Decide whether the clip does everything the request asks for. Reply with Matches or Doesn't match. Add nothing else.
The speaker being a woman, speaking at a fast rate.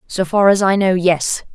Matches